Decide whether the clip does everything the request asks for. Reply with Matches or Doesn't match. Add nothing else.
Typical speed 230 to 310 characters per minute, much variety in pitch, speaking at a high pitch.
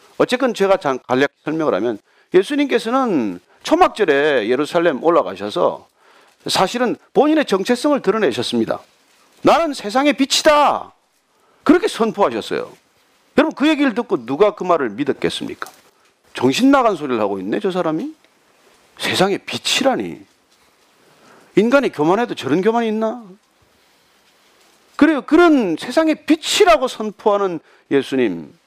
Matches